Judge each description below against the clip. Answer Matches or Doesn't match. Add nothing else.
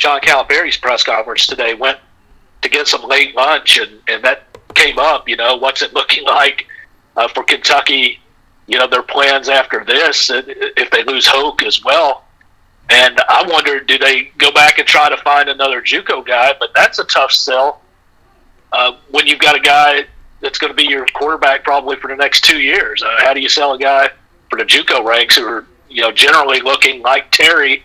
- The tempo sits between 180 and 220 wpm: Matches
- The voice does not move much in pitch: Matches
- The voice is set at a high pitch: Doesn't match